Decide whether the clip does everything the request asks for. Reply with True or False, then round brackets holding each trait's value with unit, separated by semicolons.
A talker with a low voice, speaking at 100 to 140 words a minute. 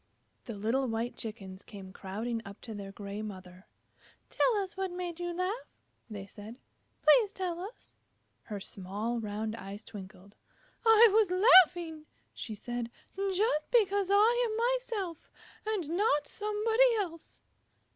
False (310 Hz; 135 wpm)